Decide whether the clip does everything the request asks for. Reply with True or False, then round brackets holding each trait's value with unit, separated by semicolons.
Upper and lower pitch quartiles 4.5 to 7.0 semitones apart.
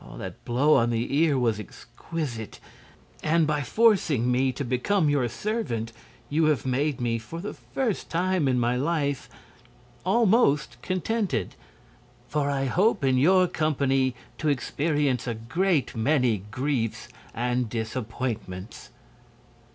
True (5.3 semitones)